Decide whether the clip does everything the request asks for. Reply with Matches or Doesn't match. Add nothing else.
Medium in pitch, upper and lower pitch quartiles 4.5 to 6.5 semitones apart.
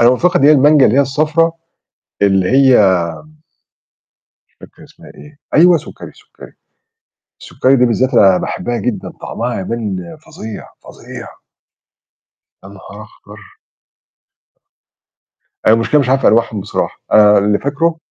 Doesn't match